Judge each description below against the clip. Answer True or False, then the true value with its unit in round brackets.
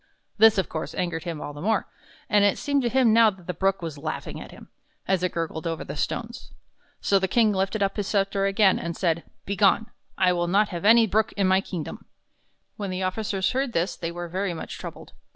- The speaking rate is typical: False (230 wpm)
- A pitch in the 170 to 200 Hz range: True (190 Hz)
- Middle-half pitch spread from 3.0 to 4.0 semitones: True (3.3 semitones)